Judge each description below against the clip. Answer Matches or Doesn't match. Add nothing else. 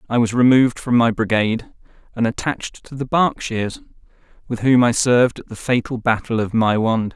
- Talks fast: Doesn't match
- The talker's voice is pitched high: Doesn't match